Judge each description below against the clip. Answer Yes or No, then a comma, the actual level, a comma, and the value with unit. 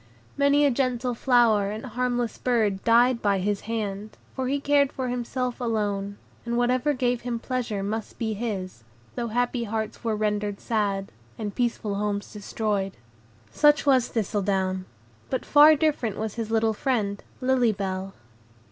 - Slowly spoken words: No, average, 150 wpm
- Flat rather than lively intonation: No, average, 3.4 semitones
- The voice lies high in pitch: Yes, high, 225 Hz